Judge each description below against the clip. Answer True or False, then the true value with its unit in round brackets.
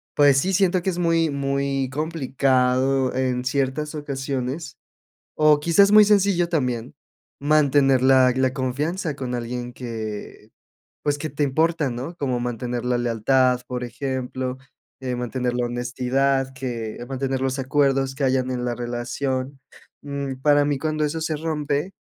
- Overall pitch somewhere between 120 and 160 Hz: True (135 Hz)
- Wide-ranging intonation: False (2.7 semitones)